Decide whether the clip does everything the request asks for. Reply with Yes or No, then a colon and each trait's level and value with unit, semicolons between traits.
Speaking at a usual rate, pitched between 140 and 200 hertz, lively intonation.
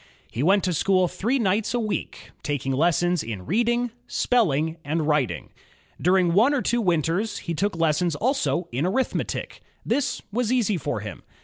Yes: average, 165 wpm; medium, 185 Hz; wide, 6.1 semitones